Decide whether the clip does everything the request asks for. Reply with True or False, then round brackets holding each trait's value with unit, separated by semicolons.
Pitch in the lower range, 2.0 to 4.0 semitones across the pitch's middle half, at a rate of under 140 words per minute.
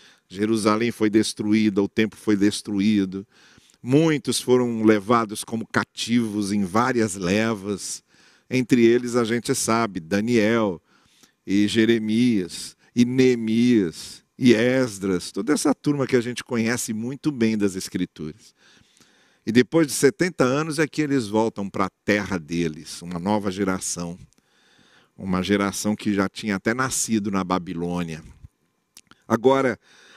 True (110 Hz; 3.6 semitones; 125 wpm)